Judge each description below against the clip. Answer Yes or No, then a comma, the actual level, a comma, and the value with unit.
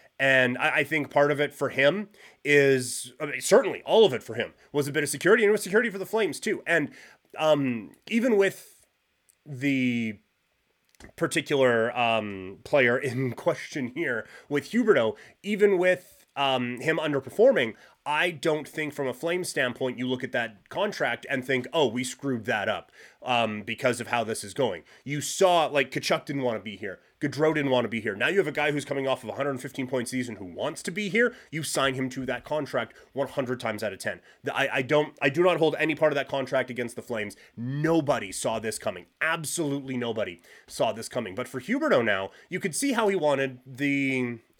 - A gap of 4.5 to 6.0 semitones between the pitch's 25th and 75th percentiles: No, average, 3.7 semitones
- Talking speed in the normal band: No, fast, 210 wpm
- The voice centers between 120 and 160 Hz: Yes, medium, 140 Hz